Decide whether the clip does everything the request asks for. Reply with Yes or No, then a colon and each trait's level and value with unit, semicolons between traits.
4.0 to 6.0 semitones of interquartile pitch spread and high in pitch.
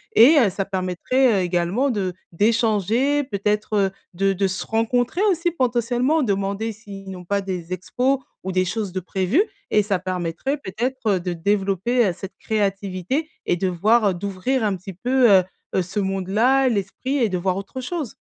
Yes: average, 4.6 semitones; high, 200 Hz